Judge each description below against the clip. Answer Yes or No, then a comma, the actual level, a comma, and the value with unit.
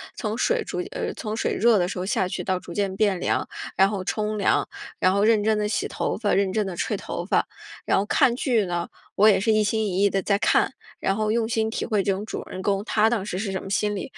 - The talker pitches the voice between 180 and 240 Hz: Yes, high, 205 Hz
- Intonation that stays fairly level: Yes, narrow, 2.2 semitones